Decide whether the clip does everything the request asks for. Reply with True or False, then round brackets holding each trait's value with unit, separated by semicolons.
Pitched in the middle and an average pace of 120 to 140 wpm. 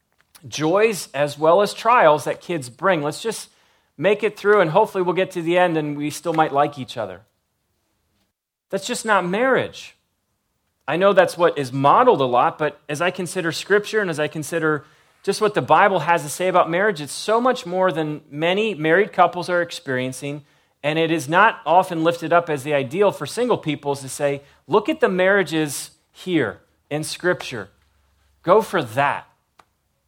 False (165 Hz; 185 wpm)